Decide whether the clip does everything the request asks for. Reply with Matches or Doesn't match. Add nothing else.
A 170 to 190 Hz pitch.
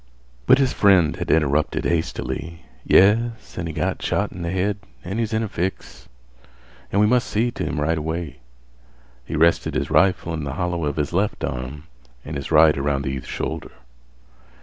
Doesn't match